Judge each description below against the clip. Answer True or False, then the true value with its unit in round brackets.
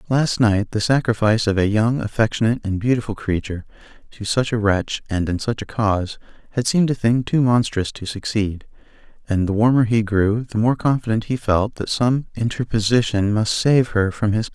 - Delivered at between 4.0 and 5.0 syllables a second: False (5.5 syllables/s)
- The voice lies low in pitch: True (110 Hz)